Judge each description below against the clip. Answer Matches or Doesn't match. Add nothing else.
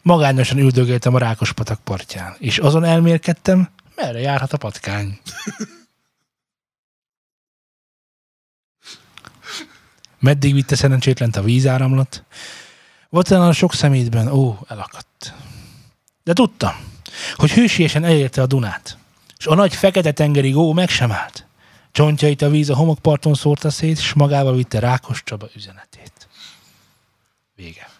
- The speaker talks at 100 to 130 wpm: Matches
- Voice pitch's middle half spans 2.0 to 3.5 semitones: Doesn't match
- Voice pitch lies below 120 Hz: Doesn't match